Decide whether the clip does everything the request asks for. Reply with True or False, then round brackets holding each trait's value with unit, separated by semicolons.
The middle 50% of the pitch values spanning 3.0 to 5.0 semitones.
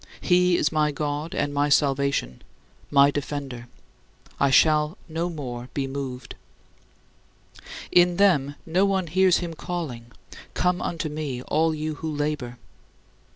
True (3.3 semitones)